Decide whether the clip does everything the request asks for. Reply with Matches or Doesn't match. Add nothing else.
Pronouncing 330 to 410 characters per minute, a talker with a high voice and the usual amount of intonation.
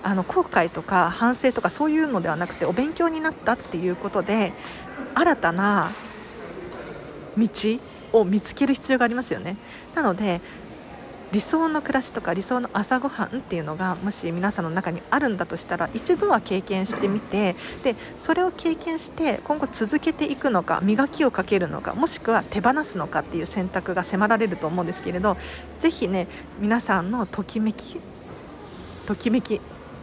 Doesn't match